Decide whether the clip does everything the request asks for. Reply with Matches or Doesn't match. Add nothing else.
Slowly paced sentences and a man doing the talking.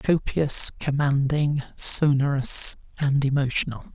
Matches